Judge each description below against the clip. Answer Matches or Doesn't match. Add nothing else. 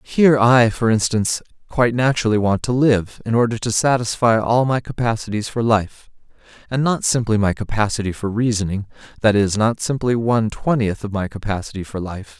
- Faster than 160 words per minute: Matches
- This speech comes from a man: Matches